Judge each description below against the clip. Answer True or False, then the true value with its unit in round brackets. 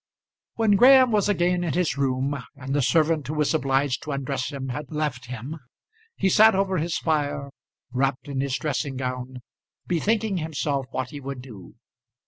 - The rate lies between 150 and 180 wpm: True (170 wpm)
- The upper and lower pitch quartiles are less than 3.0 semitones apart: False (4.3 semitones)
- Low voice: False (145 Hz)